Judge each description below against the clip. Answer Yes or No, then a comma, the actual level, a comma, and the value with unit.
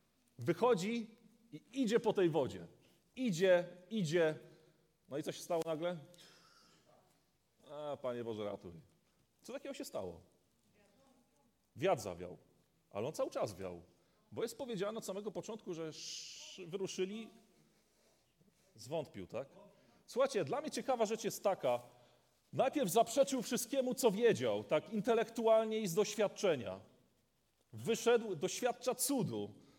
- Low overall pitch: No, medium, 185 Hz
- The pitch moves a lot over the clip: Yes, wide, 7.3 semitones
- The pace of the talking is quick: No, average, 120 wpm